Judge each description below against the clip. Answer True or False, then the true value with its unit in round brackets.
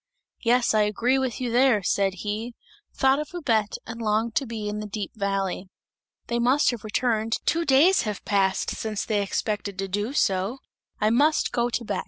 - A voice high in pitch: True (220 Hz)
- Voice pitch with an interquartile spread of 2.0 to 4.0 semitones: True (3.2 semitones)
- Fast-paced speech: False (190 wpm)